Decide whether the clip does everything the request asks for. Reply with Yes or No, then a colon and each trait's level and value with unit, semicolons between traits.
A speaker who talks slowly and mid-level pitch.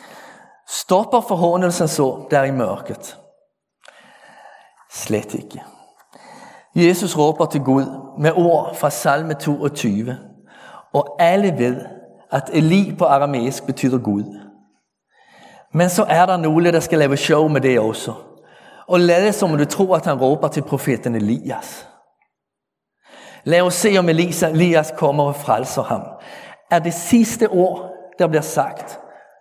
Yes: slow, 135 wpm; medium, 160 Hz